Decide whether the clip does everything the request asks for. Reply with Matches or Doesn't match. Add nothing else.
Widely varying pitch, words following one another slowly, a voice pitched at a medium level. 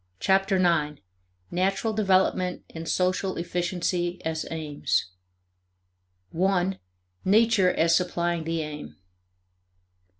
Doesn't match